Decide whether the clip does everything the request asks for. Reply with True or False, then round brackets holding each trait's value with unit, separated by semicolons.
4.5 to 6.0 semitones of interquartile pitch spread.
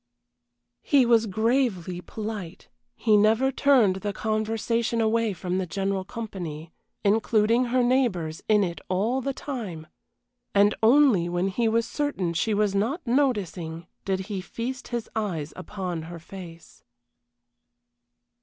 False (4.1 semitones)